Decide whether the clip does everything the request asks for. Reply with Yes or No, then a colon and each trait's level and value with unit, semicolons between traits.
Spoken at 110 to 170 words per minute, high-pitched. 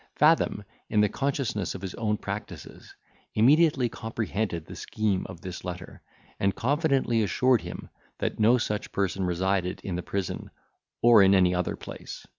No: average, 155 wpm; low, 105 Hz